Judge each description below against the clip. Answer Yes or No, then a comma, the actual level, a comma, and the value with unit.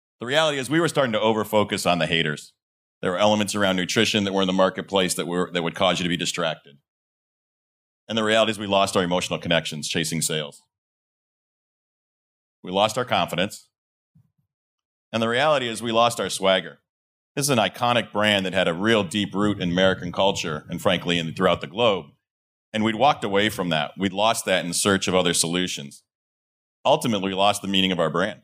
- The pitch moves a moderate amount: Yes, average, 3.5 semitones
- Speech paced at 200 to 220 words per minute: Yes, fast, 205 wpm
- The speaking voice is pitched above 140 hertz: No, very low, 95 Hz